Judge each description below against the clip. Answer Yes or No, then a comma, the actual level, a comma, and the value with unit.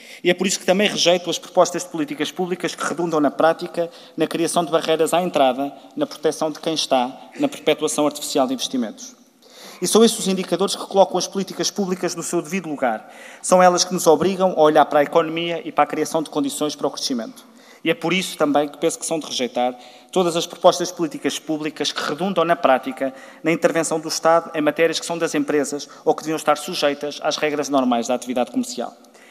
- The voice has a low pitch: No, medium, 165 Hz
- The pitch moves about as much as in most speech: Yes, average, 3.4 semitones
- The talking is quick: Yes, fast, 220 wpm